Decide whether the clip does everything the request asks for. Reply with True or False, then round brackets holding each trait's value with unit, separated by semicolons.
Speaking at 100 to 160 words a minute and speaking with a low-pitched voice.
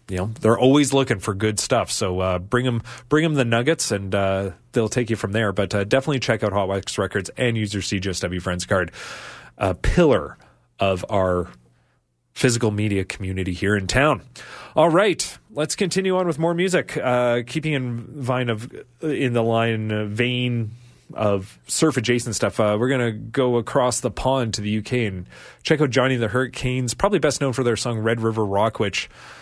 False (190 wpm; 115 Hz)